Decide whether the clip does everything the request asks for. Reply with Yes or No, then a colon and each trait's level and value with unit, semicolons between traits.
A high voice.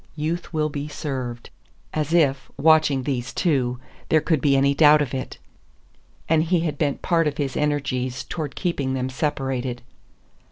No: medium, 145 Hz